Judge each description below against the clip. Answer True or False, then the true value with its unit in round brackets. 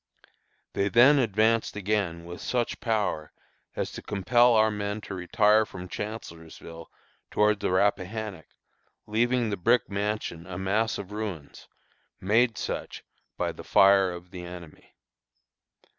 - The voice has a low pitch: True (105 Hz)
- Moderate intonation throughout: True (3.4 semitones)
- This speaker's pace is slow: True (130 wpm)